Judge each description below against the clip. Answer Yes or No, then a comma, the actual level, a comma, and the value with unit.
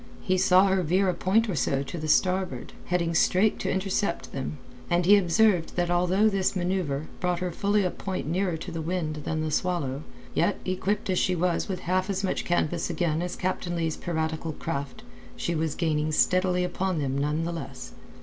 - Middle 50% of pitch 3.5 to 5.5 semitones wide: No, average, 2.7 semitones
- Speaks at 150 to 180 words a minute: No, average, 195 wpm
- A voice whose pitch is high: No, medium, 175 Hz